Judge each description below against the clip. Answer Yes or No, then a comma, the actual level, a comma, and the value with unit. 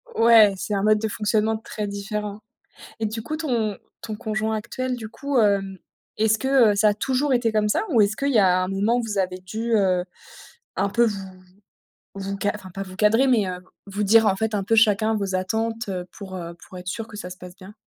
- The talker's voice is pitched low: No, high, 210 Hz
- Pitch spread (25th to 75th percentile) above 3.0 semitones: No, narrow, 2.4 semitones